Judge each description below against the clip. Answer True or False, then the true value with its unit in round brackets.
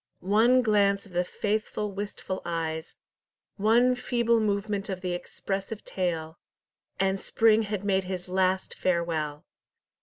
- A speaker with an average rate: False (125 wpm)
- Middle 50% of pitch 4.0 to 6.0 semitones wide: False (3.0 semitones)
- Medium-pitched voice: False (195 Hz)